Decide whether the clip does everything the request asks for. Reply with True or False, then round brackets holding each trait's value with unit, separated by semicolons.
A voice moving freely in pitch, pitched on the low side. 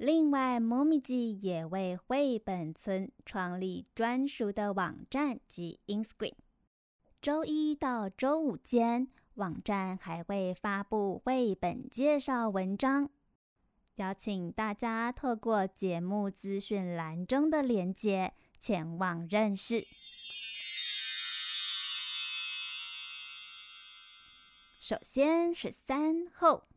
False (6.5 semitones; 205 Hz)